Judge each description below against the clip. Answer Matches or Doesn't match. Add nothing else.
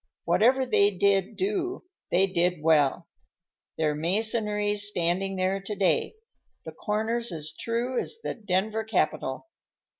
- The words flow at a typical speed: Doesn't match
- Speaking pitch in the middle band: Doesn't match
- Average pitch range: Matches